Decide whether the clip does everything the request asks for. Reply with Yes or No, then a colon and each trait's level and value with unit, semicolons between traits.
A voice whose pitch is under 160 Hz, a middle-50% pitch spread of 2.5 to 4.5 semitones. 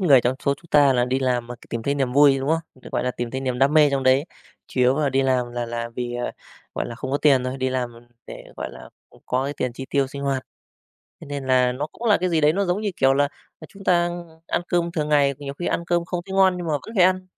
Yes: medium, 140 Hz; average, 4.2 semitones